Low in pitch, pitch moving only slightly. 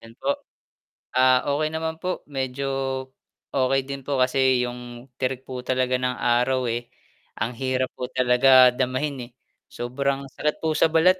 Yes: low, 130 Hz; narrow, 1.7 semitones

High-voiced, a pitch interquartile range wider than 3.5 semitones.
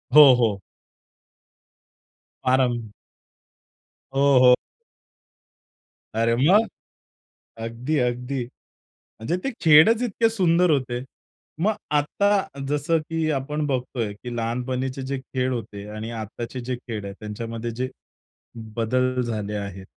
No: low, 125 Hz; average, 4.3 semitones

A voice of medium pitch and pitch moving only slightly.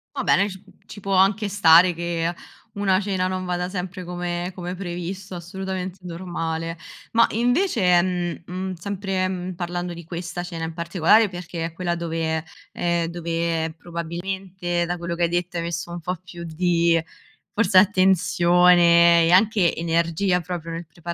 Yes: medium, 175 Hz; narrow, 1.6 semitones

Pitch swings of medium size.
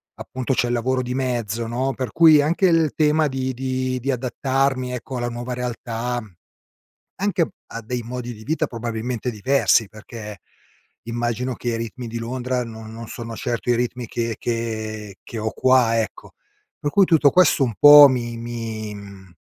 No: narrow, 2.2 semitones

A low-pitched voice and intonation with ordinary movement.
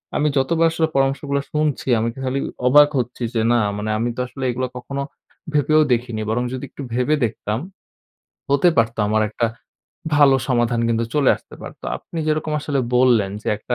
Yes: low, 130 Hz; average, 3.8 semitones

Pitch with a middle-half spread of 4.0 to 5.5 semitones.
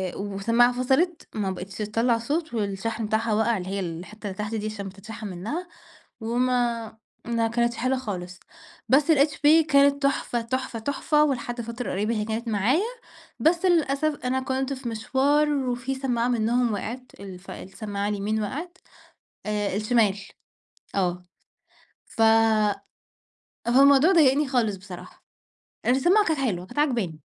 Yes: average, 4.3 semitones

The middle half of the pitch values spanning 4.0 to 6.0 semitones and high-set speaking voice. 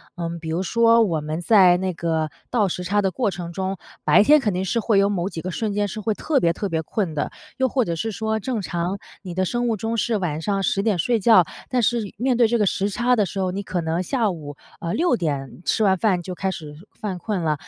Yes: average, 4.3 semitones; high, 195 Hz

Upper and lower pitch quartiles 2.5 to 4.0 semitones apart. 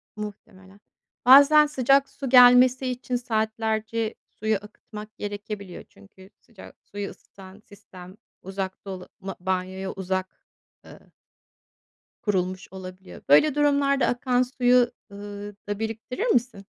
No: average, 4.5 semitones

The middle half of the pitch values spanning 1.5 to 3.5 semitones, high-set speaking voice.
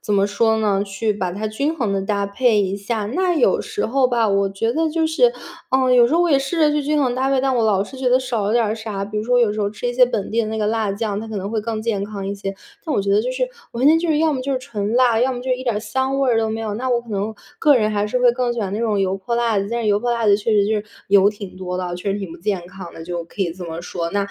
No: average, 4.0 semitones; high, 220 Hz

